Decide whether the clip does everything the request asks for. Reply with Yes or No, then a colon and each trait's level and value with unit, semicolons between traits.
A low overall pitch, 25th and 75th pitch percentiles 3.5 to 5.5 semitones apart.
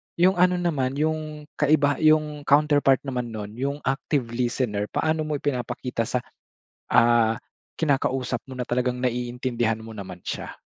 Yes: low, 130 Hz; average, 3.9 semitones